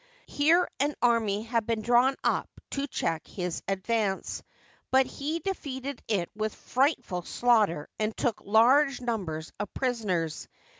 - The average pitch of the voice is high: Yes, high, 230 Hz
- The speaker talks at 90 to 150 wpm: Yes, slow, 135 wpm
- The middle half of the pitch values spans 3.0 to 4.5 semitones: No, average, 5.0 semitones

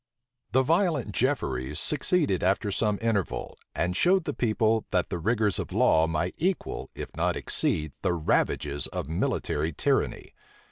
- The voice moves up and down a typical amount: No, wide, 8.3 semitones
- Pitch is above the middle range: No, low, 100 Hz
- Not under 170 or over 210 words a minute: No, average, 145 wpm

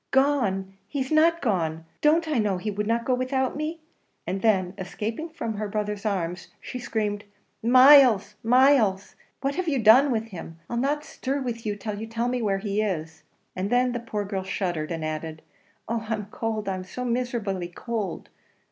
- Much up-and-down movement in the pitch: No, average, 4.7 semitones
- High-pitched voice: Yes, high, 220 Hz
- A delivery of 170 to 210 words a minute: Yes, average, 180 wpm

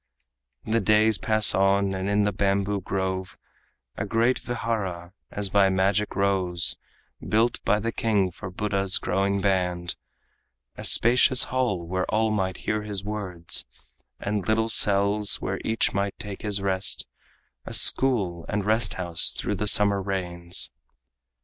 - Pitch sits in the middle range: No, low, 100 Hz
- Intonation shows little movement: Yes, narrow, 2.1 semitones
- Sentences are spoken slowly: No, average, 145 wpm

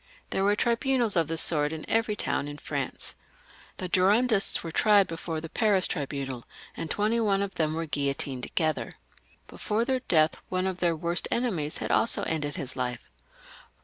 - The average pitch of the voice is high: No, medium, 175 Hz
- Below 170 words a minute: No, average, 175 wpm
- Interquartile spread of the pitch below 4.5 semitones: No, average, 5.3 semitones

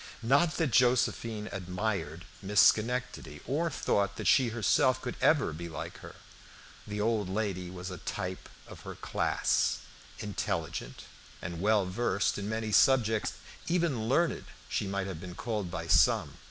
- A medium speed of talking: Yes, average, 150 wpm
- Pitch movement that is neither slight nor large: Yes, average, 4.8 semitones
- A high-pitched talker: No, low, 105 Hz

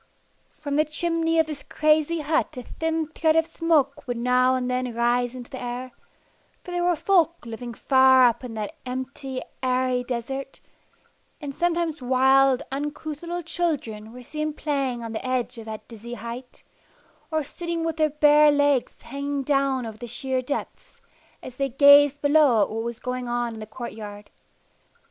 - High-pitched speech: Yes, very high, 265 Hz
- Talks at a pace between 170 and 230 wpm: Yes, average, 175 wpm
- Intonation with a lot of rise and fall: No, average, 3.8 semitones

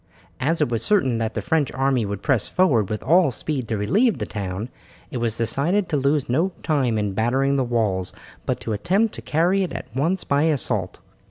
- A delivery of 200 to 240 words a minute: Yes, fast, 205 wpm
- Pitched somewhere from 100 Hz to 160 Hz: Yes, low, 135 Hz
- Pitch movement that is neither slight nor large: No, wide, 6.1 semitones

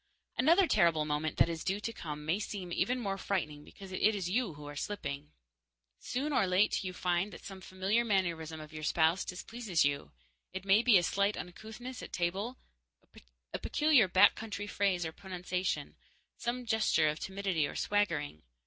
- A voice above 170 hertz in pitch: Yes, high, 190 Hz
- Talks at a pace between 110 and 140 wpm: No, average, 175 wpm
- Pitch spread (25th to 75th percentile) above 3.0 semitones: Yes, average, 4.5 semitones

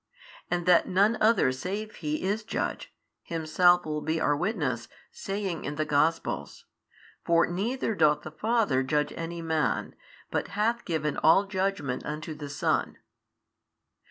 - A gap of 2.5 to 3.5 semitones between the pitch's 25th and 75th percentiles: No, average, 4.7 semitones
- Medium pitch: Yes, medium, 165 Hz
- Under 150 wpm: Yes, average, 140 wpm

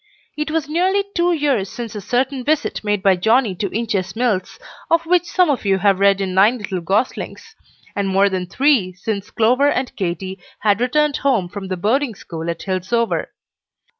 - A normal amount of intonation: No, wide, 6.4 semitones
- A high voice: Yes, high, 220 Hz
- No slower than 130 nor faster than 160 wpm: No, average, 185 wpm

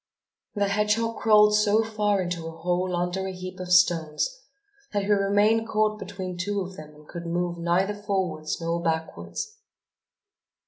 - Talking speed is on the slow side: No, average, 155 wpm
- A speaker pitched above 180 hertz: Yes, high, 190 Hz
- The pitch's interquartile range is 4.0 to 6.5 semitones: No, average, 3.4 semitones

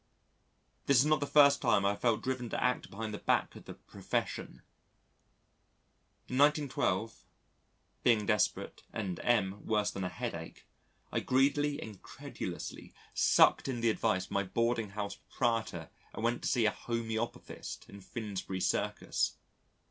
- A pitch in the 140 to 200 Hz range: No, low, 115 Hz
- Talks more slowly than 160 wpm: Yes, average, 150 wpm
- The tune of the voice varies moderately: Yes, average, 3.7 semitones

